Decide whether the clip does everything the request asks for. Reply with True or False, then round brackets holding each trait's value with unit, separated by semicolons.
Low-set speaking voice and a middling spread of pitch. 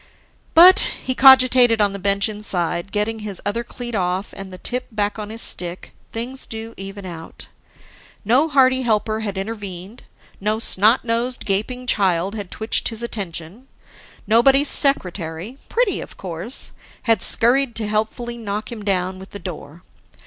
False (215 Hz; 3.7 semitones)